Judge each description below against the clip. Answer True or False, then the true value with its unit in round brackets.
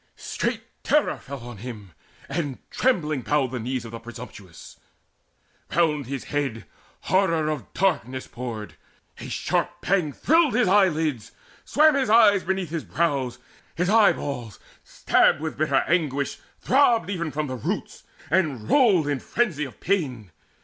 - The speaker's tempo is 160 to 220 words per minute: False (145 wpm)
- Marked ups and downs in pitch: True (6.9 semitones)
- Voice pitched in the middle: True (150 Hz)